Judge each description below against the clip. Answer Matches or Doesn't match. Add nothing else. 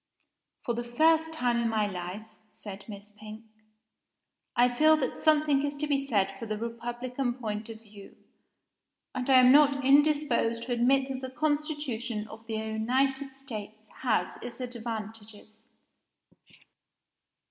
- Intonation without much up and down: Doesn't match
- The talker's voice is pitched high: Matches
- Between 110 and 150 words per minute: Matches